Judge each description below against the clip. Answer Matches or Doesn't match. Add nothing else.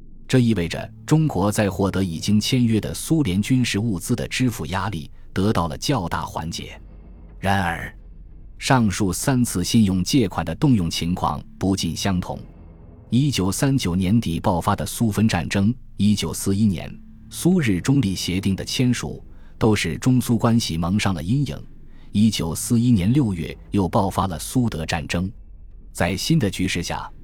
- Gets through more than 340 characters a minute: Doesn't match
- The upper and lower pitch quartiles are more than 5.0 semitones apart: Matches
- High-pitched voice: Doesn't match